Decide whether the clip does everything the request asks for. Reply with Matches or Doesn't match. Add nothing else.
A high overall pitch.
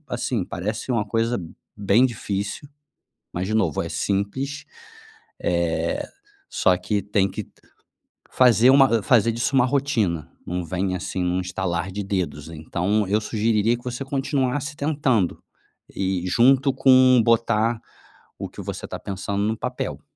Doesn't match